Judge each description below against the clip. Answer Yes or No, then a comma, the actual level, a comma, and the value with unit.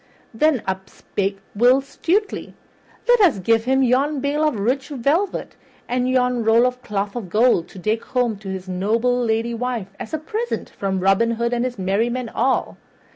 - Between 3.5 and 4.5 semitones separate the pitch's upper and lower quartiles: Yes, average, 3.9 semitones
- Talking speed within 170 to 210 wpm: Yes, average, 180 wpm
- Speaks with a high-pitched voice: Yes, high, 240 Hz